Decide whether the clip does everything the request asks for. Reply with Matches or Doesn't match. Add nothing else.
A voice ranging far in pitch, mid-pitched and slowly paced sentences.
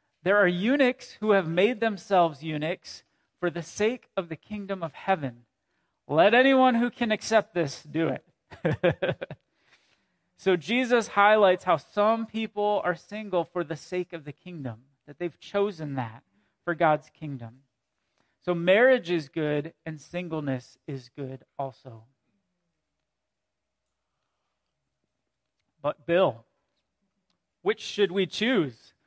Matches